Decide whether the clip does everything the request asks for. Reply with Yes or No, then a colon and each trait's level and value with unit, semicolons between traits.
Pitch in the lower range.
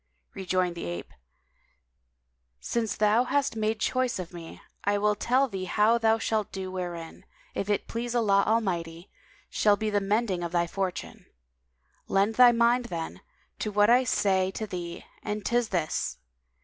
No: high, 205 Hz